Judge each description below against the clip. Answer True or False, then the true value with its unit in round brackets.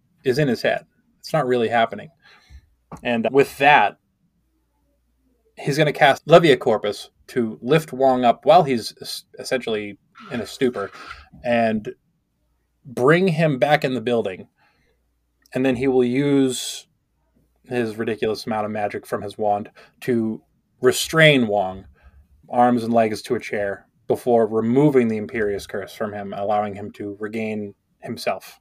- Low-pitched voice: True (115 Hz)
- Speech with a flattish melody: False (3.9 semitones)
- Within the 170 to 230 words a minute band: False (145 wpm)